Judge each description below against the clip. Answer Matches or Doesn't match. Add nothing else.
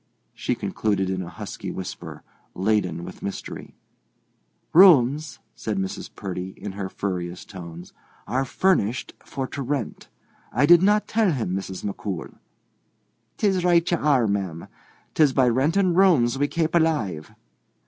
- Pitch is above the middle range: Doesn't match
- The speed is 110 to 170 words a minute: Matches